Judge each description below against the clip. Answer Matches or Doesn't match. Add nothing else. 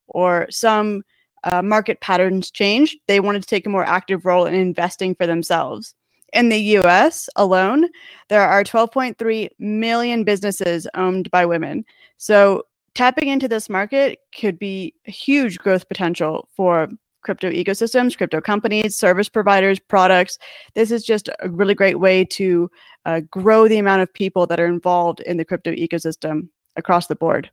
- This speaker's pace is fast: Doesn't match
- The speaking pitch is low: Doesn't match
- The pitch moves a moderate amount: Matches